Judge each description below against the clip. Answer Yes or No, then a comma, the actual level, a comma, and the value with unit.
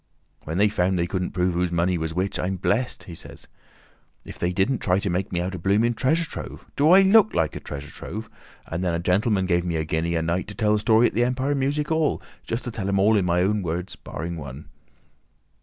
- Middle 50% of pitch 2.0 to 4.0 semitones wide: No, average, 4.6 semitones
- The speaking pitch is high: No, very low, 95 Hz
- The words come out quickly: Yes, fast, 230 wpm